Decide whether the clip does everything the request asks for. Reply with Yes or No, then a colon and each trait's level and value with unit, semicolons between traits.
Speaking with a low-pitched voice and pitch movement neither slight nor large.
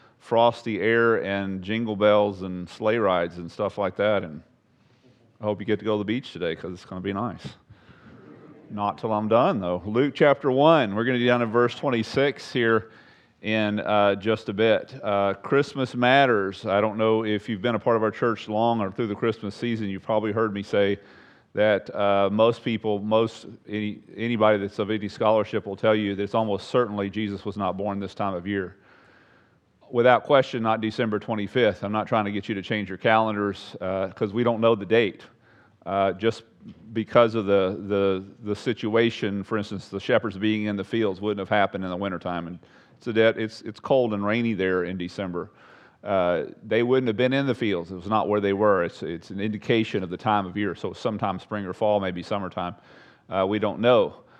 No: low, 105 Hz; narrow, 2.2 semitones